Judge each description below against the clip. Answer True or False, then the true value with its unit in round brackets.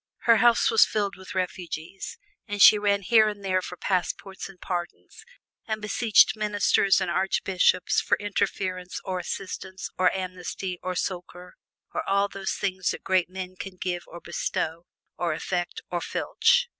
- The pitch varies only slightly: True (2.0 semitones)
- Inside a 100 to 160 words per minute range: True (155 wpm)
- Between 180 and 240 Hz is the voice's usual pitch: True (190 Hz)